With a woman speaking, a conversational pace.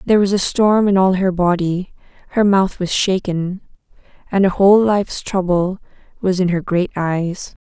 Yes: female; average, 175 wpm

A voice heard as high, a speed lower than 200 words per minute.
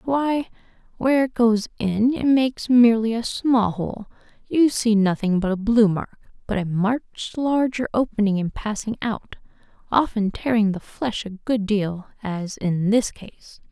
Yes: high, 220 Hz; average, 160 wpm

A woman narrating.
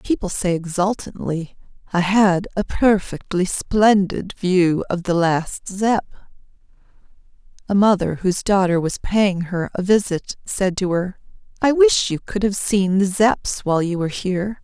Yes: female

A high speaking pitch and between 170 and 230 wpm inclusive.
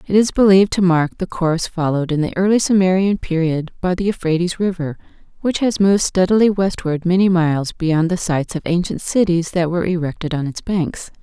No: medium, 175 Hz; average, 190 wpm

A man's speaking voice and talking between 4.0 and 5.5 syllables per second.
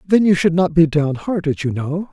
Yes: male; 5.0 syllables/s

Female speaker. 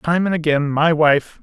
No: male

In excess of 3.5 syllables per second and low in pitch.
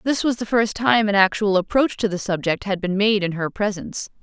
No: 5.5 syllables/s; high, 205 Hz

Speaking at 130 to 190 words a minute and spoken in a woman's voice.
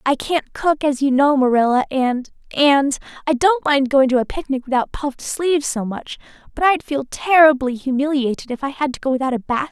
No: average, 200 wpm; female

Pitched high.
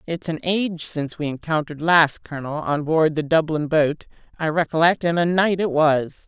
No: medium, 160 Hz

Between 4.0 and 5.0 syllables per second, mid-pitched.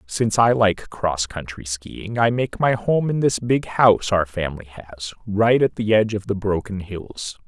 No: 4.5 syllables/s; low, 105 Hz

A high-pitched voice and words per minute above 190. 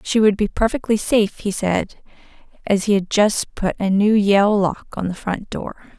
Yes: high, 205 Hz; average, 200 wpm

